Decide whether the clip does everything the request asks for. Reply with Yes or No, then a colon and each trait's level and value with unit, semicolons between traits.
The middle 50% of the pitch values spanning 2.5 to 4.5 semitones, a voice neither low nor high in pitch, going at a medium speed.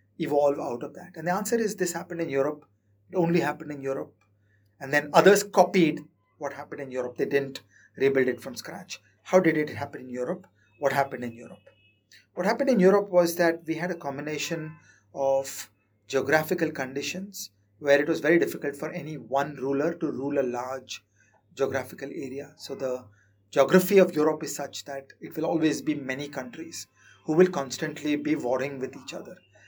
Yes: average, 3.9 semitones; medium, 145 Hz; average, 185 wpm